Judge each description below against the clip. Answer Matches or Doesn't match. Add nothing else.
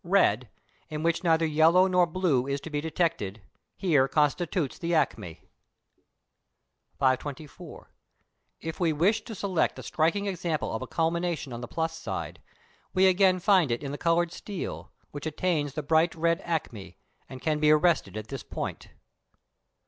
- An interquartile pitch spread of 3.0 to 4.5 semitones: Matches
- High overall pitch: Doesn't match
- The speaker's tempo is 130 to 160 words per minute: Matches